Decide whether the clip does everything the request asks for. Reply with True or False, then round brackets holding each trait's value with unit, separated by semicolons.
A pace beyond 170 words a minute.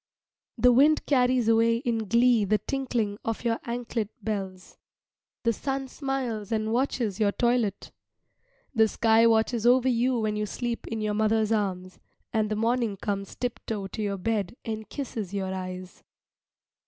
False (155 wpm)